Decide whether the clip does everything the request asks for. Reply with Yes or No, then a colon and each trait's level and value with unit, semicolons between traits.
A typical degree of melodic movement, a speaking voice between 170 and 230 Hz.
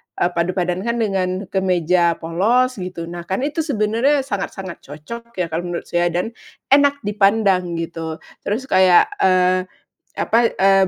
Yes: average, 4.4 semitones; medium, 185 Hz